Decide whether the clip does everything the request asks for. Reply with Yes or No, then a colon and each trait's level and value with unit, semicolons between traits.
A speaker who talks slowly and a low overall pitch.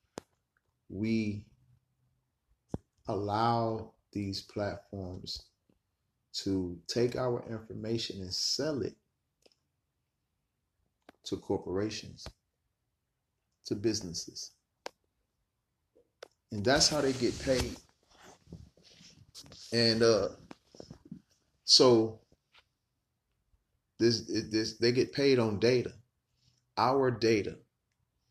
Yes: slow, 70 wpm; low, 115 Hz